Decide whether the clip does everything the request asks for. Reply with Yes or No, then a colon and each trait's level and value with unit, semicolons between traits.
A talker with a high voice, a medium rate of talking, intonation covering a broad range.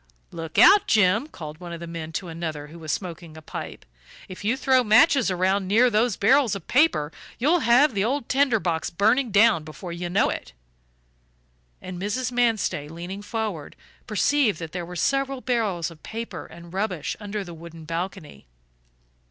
Yes: high, 195 Hz; average, 175 wpm; wide, 5.9 semitones